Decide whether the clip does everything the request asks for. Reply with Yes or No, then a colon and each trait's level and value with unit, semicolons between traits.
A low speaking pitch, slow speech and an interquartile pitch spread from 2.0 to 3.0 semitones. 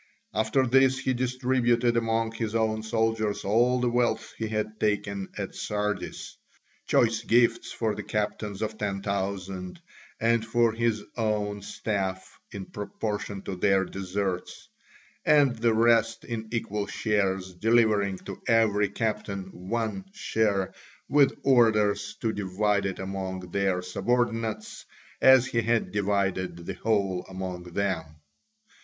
Yes: low, 105 Hz; slow, 130 wpm; average, 2.7 semitones